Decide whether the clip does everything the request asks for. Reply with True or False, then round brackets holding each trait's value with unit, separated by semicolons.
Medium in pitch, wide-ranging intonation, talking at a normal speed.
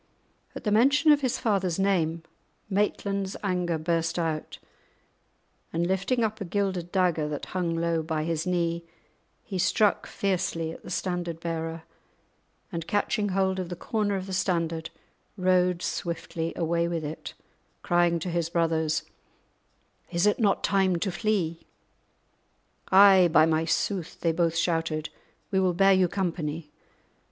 False (175 Hz; 2.7 semitones; 145 wpm)